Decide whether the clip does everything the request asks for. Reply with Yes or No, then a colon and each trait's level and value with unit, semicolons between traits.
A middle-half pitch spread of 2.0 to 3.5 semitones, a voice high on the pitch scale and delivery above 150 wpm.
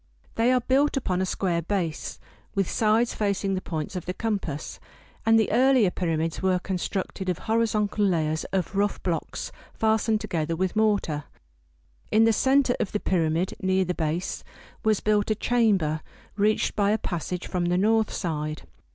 No: average, 3.9 semitones; high, 195 Hz; average, 165 wpm